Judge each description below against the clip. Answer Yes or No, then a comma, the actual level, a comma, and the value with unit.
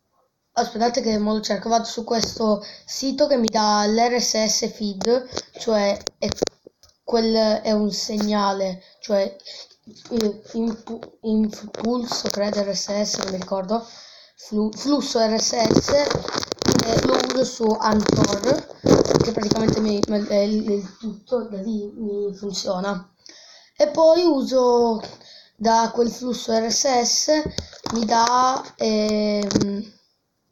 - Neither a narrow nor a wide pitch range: No, narrow, 2.3 semitones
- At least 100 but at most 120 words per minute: Yes, slow, 115 wpm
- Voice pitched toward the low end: No, high, 220 Hz